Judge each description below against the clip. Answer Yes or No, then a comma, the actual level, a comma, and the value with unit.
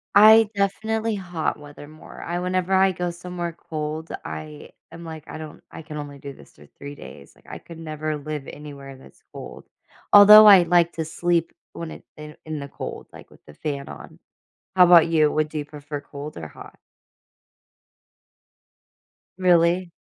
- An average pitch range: Yes, average, 3.3 semitones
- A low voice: No, medium, 160 Hz